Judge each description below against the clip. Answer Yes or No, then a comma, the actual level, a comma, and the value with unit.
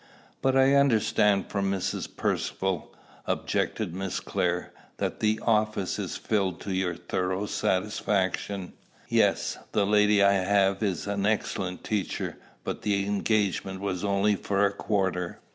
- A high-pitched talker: No, low, 100 Hz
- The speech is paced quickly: No, slow, 135 wpm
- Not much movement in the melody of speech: Yes, narrow, 1.8 semitones